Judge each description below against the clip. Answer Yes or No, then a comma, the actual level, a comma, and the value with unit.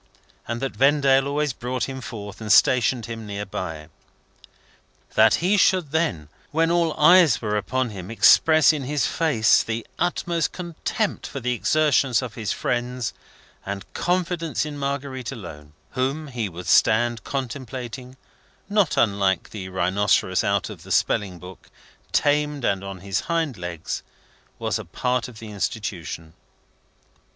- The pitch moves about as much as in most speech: No, wide, 6.2 semitones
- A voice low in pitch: Yes, low, 125 Hz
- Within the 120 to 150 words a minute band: Yes, average, 145 wpm